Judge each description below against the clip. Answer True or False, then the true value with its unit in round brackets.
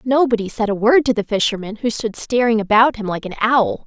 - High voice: True (225 Hz)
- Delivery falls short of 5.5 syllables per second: False (5.7 syllables/s)